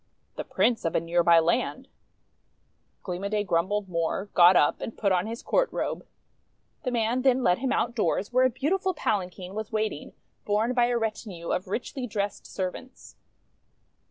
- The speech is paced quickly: No, average, 170 wpm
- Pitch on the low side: No, high, 210 Hz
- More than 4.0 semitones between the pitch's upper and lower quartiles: Yes, average, 5.2 semitones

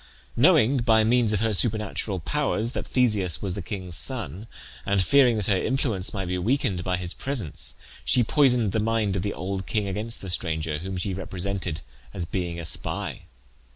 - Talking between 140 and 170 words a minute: No, average, 185 wpm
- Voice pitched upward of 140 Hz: No, low, 100 Hz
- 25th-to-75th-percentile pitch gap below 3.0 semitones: No, average, 4.1 semitones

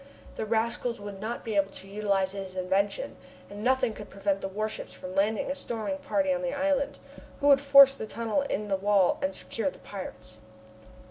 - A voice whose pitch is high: Yes, high, 215 Hz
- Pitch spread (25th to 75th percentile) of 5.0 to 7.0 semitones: Yes, average, 5.3 semitones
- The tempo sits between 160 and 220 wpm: Yes, average, 195 wpm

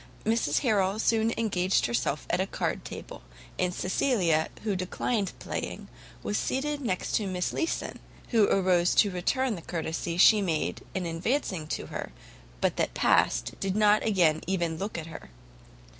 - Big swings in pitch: No, average, 4.2 semitones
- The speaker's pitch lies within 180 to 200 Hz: Yes, high, 190 Hz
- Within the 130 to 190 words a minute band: Yes, average, 160 wpm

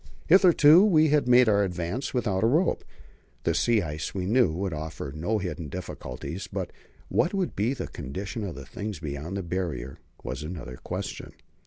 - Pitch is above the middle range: No, very low, 95 Hz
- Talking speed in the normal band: Yes, average, 170 wpm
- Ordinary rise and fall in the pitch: No, wide, 7.7 semitones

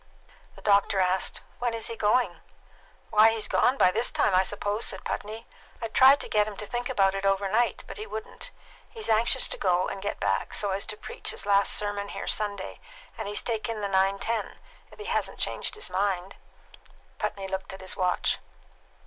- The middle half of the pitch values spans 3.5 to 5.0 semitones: No, average, 2.8 semitones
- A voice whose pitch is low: No, high, 205 Hz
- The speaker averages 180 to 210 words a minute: Yes, average, 195 wpm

